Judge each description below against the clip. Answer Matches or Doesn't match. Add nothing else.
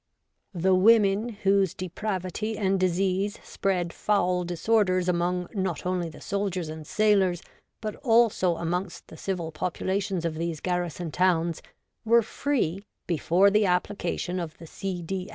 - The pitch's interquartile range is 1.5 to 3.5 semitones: Matches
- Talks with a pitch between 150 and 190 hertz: Matches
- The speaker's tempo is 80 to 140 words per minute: Matches